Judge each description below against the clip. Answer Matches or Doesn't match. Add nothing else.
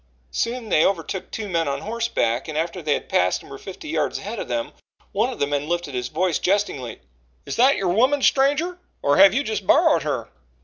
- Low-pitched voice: Doesn't match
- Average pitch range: Doesn't match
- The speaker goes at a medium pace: Doesn't match